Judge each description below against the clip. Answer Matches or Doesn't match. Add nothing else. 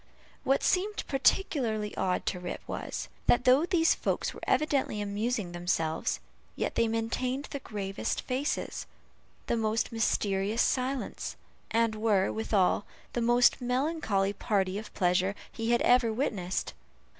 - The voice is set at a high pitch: Matches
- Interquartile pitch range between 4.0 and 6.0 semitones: Matches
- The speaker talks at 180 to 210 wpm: Doesn't match